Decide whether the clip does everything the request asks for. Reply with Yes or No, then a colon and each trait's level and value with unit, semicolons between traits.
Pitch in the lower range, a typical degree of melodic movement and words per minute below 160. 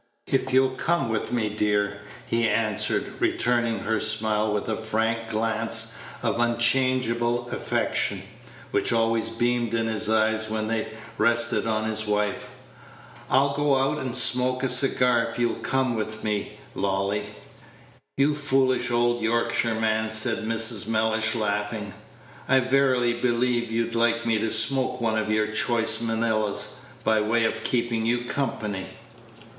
No: low, 115 Hz; narrow, 1.8 semitones; average, 140 wpm